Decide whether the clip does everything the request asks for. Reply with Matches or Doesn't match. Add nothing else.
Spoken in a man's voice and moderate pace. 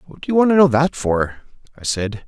Doesn't match